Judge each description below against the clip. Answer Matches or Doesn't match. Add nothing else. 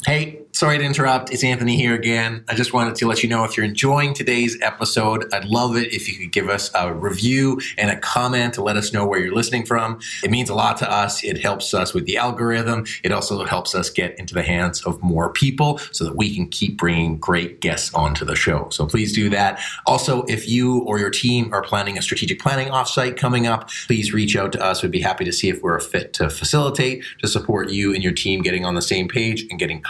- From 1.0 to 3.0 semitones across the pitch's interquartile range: Doesn't match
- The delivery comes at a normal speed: Doesn't match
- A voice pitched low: Matches